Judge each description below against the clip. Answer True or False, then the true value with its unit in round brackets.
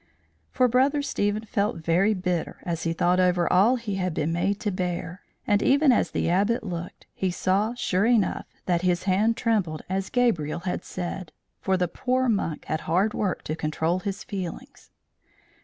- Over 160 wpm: True (175 wpm)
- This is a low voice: False (185 Hz)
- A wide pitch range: False (3.8 semitones)